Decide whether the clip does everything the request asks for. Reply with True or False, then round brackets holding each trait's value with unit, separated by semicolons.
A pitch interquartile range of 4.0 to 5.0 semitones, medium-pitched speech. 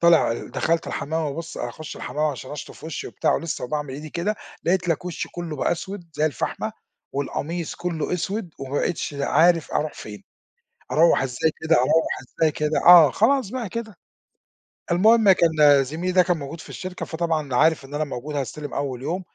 False (3.3 semitones; 160 Hz)